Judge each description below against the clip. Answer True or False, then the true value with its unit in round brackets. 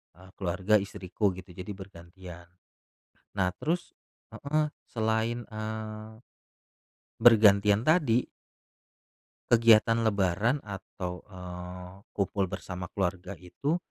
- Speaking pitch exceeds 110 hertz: False (100 Hz)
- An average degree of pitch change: True (3.6 semitones)